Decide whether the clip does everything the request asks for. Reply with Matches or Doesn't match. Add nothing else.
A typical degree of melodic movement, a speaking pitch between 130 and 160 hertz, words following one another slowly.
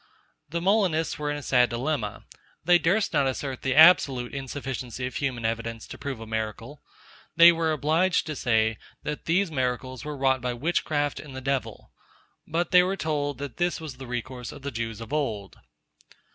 Doesn't match